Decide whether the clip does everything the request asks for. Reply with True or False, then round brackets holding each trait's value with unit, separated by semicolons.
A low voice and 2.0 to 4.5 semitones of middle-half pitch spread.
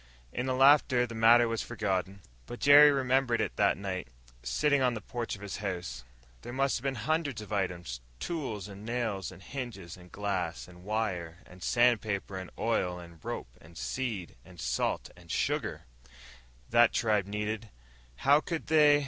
False (110 Hz; 5.3 semitones)